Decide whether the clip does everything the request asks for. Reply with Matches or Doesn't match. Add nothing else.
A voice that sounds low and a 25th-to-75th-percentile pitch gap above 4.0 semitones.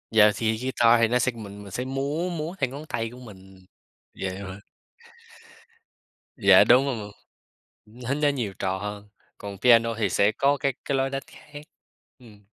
Matches